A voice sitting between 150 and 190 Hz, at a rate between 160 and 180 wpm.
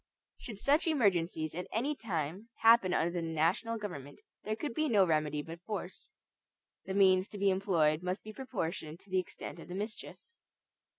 Yes: medium, 185 Hz; average, 175 wpm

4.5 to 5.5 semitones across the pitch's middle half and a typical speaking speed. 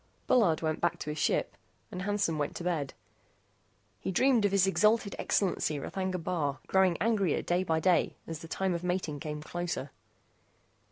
No: average, 3.4 semitones; average, 170 wpm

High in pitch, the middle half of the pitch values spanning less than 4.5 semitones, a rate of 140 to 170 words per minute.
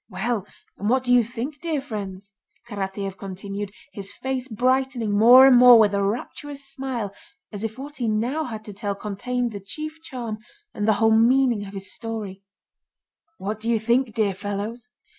No: high, 225 Hz; average, 3.7 semitones; average, 180 wpm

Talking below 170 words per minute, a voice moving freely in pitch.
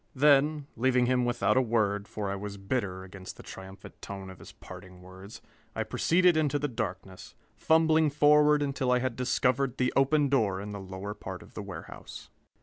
No: average, 185 wpm; wide, 6.1 semitones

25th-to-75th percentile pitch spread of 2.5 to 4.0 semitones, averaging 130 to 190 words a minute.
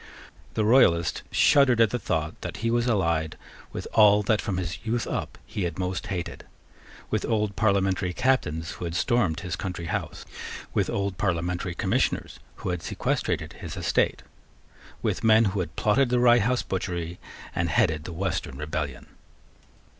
No: average, 4.7 semitones; average, 160 wpm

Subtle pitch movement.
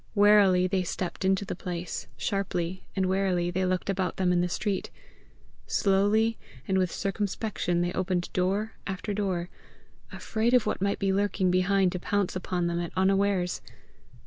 Yes: narrow, 1.8 semitones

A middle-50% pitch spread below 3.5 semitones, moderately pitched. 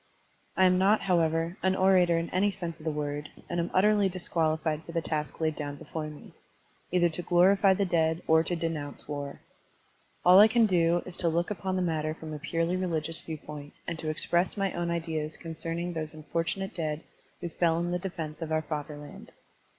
Yes: narrow, 2.5 semitones; medium, 165 Hz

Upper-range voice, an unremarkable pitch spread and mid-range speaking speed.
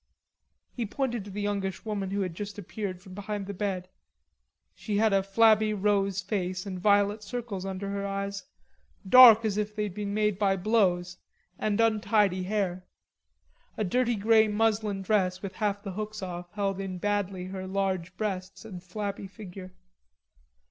No: high, 200 Hz; narrow, 2.1 semitones; average, 160 wpm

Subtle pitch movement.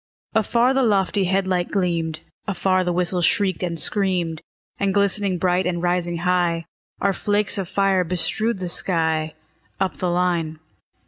Yes: narrow, 2.2 semitones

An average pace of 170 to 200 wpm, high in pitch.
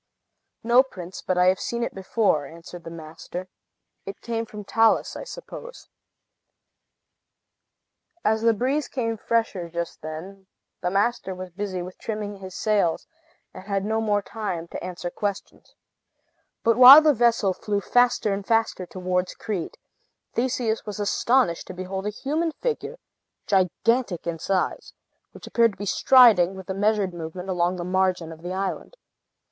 No: average, 155 wpm; high, 195 Hz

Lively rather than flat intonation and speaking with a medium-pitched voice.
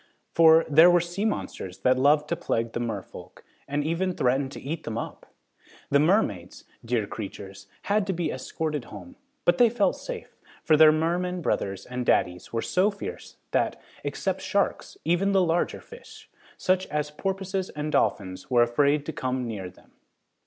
Yes: wide, 7.1 semitones; medium, 150 Hz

